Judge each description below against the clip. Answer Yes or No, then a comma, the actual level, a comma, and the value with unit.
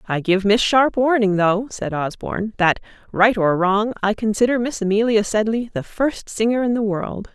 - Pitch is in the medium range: No, high, 215 Hz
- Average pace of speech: Yes, average, 190 wpm